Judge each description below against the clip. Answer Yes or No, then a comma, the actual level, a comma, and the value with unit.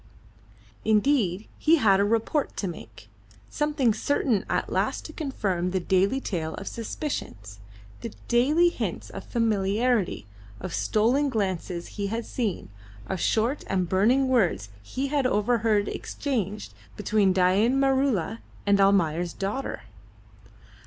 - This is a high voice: Yes, high, 210 Hz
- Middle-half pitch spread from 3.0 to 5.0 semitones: No, wide, 5.5 semitones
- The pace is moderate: No, slow, 125 wpm